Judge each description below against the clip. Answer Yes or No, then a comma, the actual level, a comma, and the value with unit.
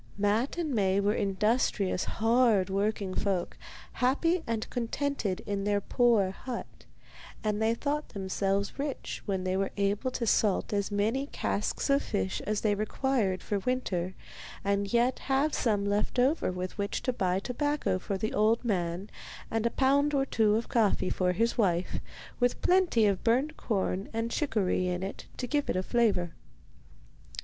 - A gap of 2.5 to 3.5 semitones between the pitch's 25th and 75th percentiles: No, average, 4.2 semitones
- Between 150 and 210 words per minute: Yes, average, 165 wpm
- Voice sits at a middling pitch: No, high, 215 Hz